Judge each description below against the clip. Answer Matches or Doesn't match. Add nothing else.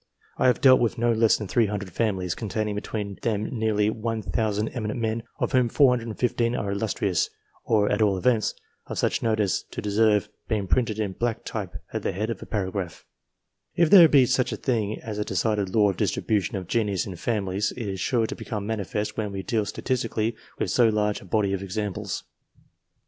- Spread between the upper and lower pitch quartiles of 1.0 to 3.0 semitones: Matches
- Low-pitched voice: Matches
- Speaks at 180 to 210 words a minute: Matches